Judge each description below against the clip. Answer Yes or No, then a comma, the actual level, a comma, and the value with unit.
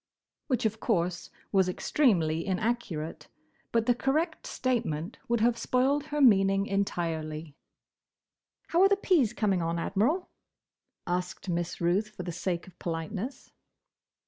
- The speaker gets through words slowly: Yes, slow, 130 wpm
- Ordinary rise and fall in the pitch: No, wide, 6.0 semitones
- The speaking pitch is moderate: No, high, 200 Hz